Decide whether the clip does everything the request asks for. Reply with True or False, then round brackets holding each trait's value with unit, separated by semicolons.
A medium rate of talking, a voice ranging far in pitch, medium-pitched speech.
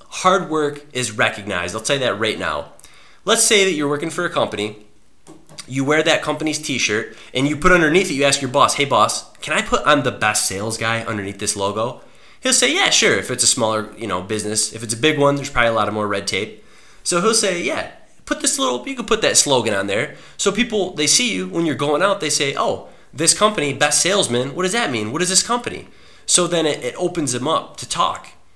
False (245 wpm; 8.3 semitones; 145 Hz)